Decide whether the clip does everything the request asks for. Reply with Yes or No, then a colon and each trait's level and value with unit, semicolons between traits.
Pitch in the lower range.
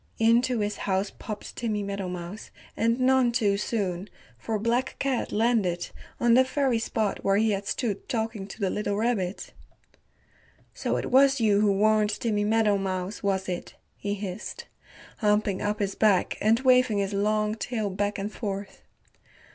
No: high, 210 Hz